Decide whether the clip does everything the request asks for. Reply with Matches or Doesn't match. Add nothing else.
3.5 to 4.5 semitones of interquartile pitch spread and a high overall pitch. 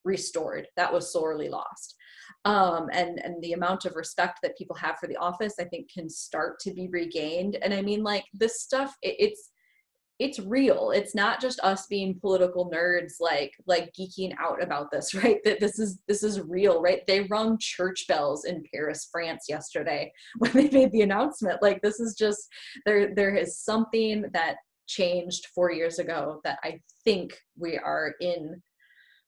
Matches